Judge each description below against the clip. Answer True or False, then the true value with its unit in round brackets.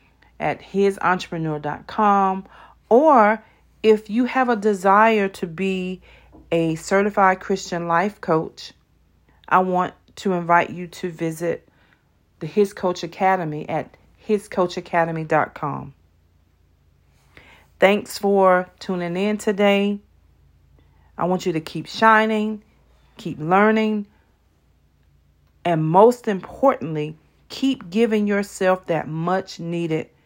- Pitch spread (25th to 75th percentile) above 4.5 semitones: True (4.9 semitones)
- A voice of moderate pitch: True (180 Hz)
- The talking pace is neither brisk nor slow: False (100 wpm)